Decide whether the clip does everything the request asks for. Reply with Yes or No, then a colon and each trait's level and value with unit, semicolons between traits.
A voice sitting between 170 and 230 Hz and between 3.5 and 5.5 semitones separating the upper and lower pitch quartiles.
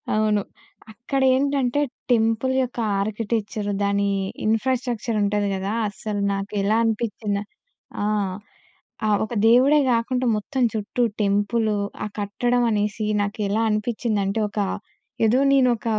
No: high, 220 Hz; average, 2.9 semitones